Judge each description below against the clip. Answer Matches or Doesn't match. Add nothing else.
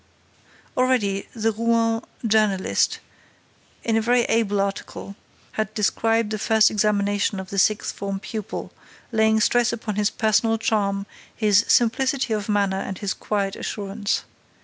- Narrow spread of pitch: Matches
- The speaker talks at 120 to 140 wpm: Matches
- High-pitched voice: Matches